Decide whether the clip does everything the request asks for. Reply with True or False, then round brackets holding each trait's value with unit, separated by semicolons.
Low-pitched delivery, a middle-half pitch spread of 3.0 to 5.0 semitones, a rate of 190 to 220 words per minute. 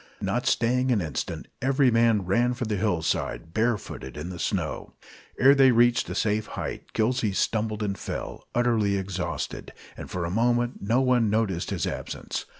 False (110 Hz; 3.8 semitones; 165 wpm)